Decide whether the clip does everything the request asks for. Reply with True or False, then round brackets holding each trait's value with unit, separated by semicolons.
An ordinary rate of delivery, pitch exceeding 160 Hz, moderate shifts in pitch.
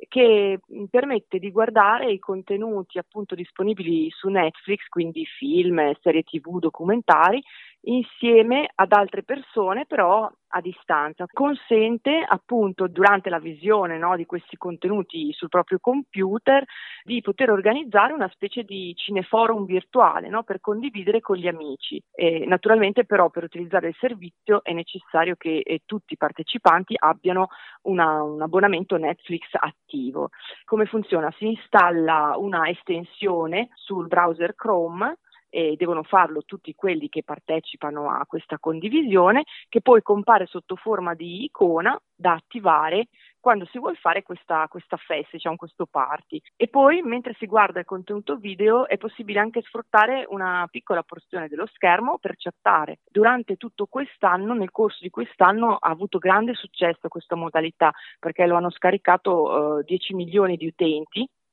True (145 wpm; 190 Hz; 4.5 semitones)